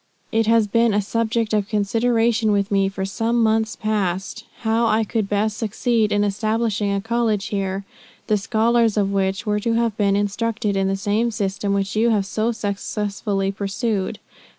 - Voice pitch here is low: No, high, 210 Hz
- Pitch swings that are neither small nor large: No, narrow, 2.3 semitones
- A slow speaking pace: No, average, 175 wpm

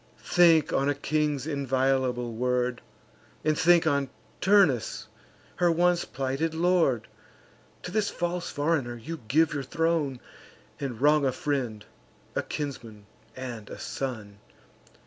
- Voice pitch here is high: No, medium, 140 Hz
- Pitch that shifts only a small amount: No, average, 4.5 semitones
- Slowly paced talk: Yes, slow, 125 wpm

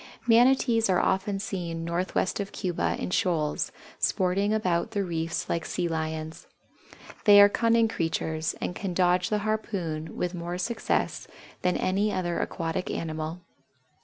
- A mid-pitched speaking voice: Yes, medium, 180 Hz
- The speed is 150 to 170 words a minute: No, average, 140 wpm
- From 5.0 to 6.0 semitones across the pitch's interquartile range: No, average, 3.5 semitones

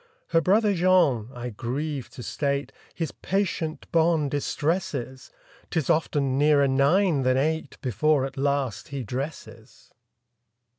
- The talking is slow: Yes, slow, 115 wpm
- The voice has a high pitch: No, medium, 140 Hz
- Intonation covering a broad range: No, average, 3.6 semitones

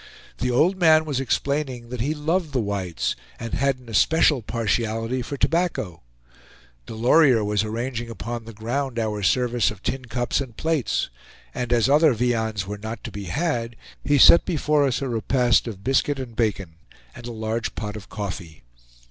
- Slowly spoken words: No, average, 175 wpm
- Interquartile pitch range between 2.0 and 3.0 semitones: No, average, 3.9 semitones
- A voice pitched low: Yes, low, 120 Hz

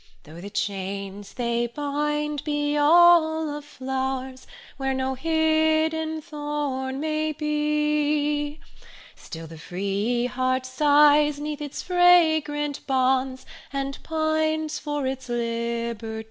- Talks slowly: Yes, slow, 105 wpm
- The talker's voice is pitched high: Yes, very high, 290 Hz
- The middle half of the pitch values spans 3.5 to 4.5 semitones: No, average, 2.9 semitones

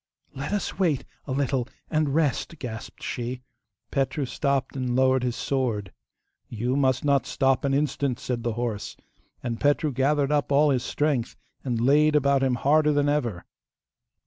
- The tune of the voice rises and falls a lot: No, average, 2.7 semitones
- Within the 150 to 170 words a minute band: Yes, average, 160 wpm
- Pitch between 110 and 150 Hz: Yes, low, 135 Hz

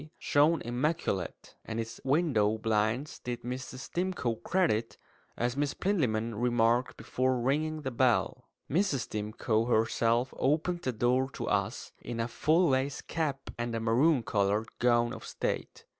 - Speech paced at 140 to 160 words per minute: Yes, average, 145 wpm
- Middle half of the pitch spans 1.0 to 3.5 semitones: No, average, 4.2 semitones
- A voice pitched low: Yes, low, 125 Hz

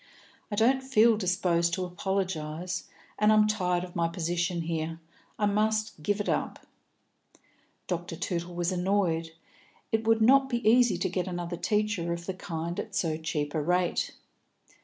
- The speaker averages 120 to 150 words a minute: No, average, 160 wpm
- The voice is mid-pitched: Yes, medium, 180 Hz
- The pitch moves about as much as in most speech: Yes, average, 3.8 semitones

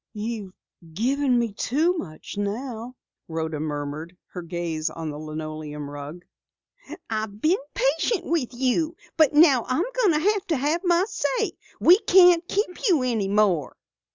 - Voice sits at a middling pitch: No, high, 235 Hz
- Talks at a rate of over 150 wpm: No, average, 140 wpm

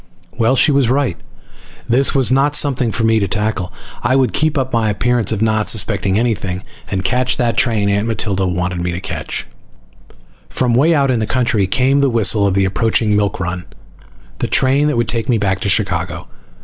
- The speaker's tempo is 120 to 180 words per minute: No, average, 200 wpm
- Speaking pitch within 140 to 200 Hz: No, low, 115 Hz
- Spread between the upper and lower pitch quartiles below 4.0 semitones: No, average, 4.5 semitones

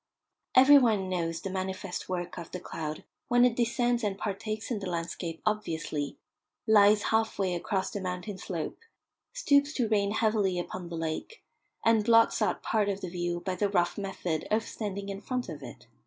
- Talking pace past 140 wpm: Yes, average, 185 wpm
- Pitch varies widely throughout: No, average, 3.8 semitones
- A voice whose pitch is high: Yes, high, 200 Hz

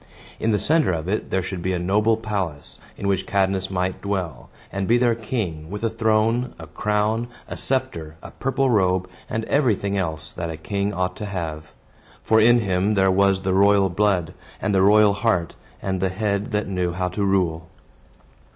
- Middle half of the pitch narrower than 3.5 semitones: Yes, average, 2.8 semitones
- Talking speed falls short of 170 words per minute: No, average, 190 wpm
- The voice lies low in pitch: Yes, low, 100 Hz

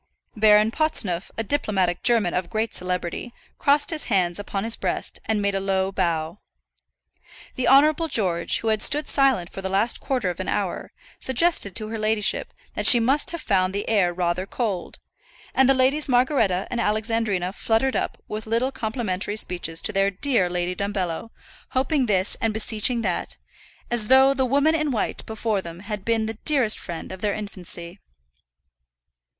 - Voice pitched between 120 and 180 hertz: No, high, 215 Hz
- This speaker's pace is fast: No, average, 170 wpm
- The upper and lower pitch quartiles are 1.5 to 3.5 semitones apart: No, average, 4.8 semitones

